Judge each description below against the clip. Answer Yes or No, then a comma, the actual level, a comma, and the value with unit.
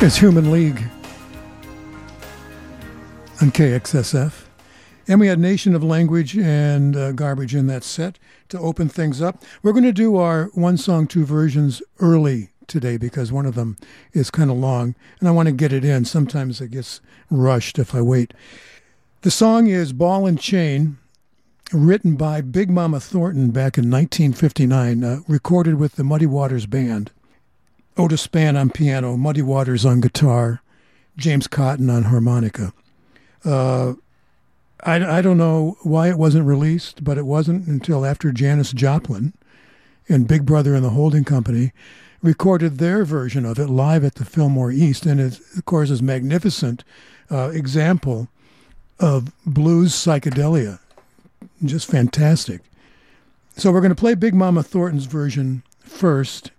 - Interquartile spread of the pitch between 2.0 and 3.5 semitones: No, average, 4.3 semitones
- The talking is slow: No, average, 155 wpm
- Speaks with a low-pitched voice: No, medium, 145 Hz